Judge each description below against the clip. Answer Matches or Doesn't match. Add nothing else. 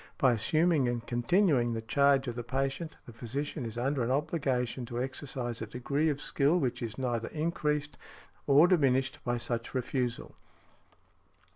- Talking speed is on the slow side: Doesn't match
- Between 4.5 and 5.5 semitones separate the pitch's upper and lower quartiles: Doesn't match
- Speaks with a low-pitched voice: Matches